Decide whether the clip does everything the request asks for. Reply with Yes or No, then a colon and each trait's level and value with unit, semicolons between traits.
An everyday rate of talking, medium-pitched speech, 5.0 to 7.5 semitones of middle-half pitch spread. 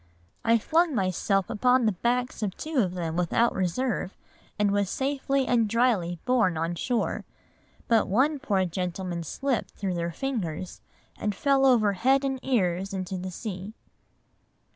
No: average, 150 wpm; high, 210 Hz; wide, 5.6 semitones